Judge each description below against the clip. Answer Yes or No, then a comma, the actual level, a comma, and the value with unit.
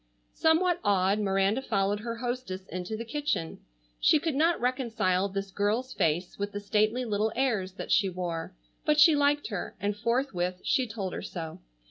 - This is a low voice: No, high, 210 Hz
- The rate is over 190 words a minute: No, average, 170 wpm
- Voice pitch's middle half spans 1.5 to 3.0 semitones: No, average, 5.1 semitones